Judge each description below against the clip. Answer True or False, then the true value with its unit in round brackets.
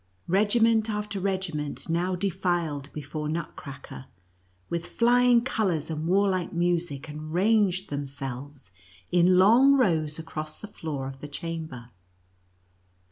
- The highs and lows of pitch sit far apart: False (5.0 semitones)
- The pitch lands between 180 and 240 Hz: False (170 Hz)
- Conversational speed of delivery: False (115 wpm)